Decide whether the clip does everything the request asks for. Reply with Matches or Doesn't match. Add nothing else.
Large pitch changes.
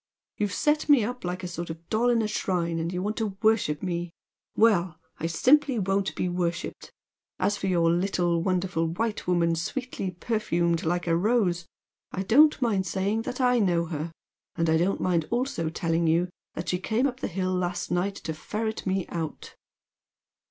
Doesn't match